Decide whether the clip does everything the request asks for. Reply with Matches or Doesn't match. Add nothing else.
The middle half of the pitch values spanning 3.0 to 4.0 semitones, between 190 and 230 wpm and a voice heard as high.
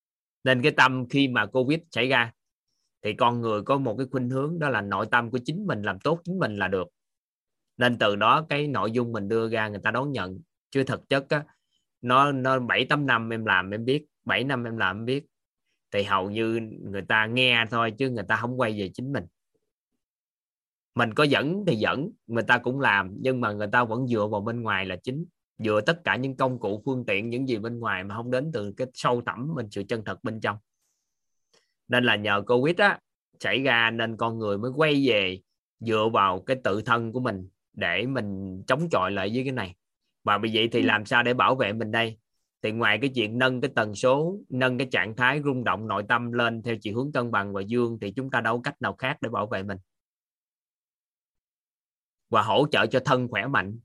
Doesn't match